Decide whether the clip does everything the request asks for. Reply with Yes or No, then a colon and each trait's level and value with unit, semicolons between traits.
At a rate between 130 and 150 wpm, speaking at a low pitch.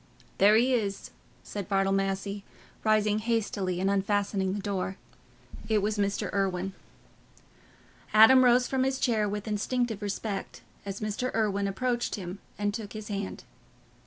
No: average, 140 wpm; high, 205 Hz